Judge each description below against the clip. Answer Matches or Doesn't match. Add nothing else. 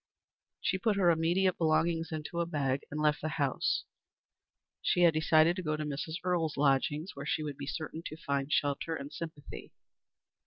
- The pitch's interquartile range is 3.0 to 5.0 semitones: Doesn't match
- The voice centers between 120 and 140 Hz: Doesn't match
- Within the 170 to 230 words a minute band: Matches